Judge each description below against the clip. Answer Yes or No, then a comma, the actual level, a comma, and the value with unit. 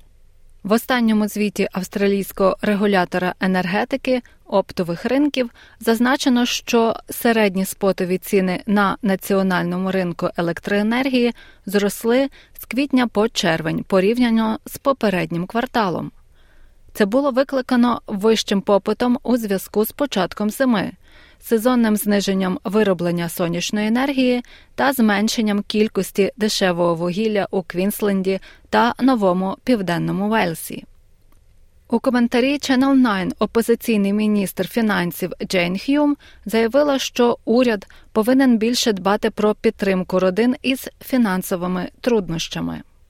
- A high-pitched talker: Yes, high, 210 Hz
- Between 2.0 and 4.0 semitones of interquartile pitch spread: No, average, 4.4 semitones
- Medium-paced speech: No, slow, 100 wpm